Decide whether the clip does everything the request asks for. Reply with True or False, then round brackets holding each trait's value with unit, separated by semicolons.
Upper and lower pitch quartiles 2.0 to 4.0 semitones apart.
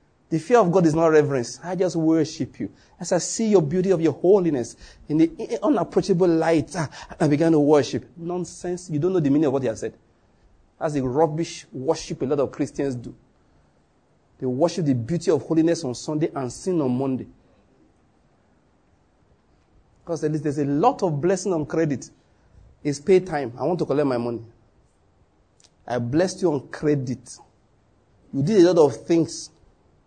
False (5.2 semitones)